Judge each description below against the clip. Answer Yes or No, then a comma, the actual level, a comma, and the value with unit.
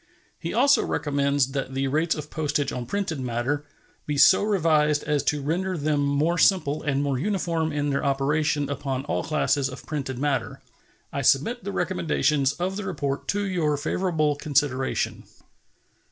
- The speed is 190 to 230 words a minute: No, average, 160 wpm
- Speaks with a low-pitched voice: No, medium, 150 Hz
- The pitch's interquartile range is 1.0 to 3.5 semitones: Yes, average, 2.9 semitones